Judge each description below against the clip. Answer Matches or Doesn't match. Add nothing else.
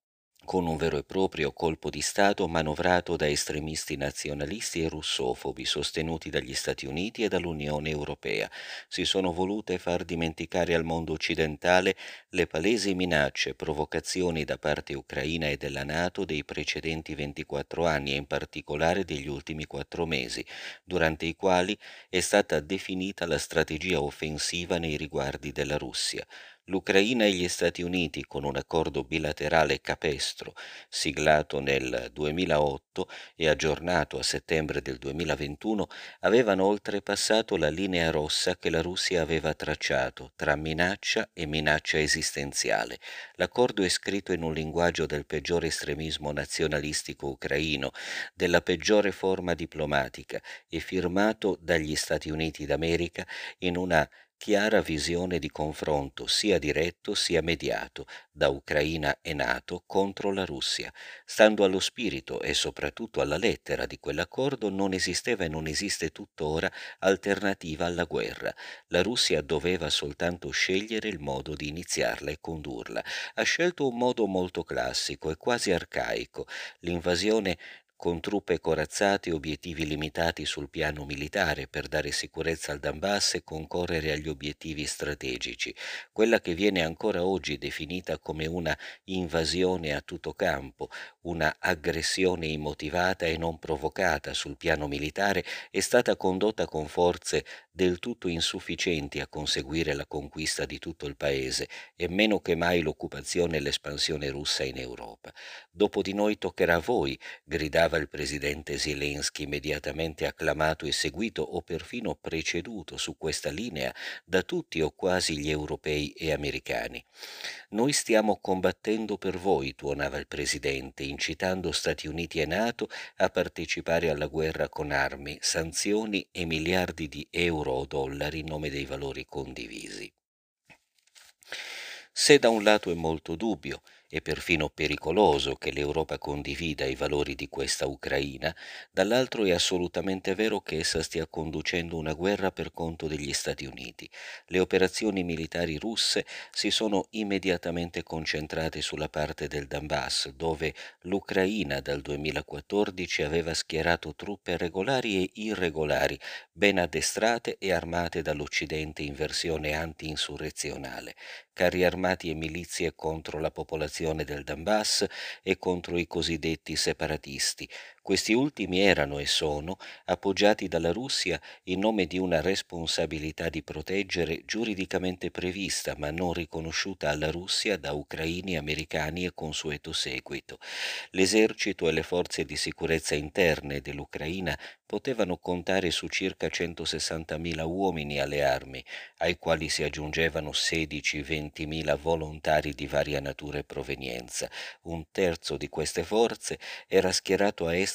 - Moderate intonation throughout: Matches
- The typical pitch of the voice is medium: Doesn't match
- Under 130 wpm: Doesn't match